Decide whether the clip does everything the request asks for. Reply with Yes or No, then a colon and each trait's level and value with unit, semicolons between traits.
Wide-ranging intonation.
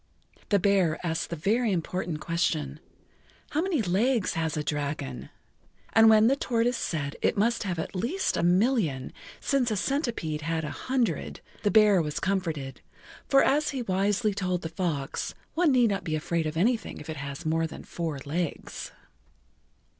Yes: wide, 6.3 semitones